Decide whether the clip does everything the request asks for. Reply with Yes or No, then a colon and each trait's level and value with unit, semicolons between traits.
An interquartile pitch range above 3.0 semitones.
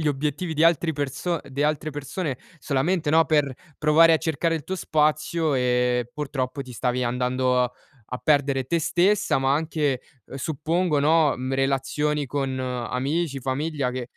Yes: average, 3.4 semitones